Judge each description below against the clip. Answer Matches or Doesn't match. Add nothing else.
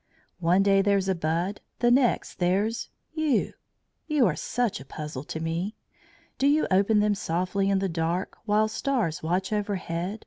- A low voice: Doesn't match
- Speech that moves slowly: Doesn't match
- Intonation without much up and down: Doesn't match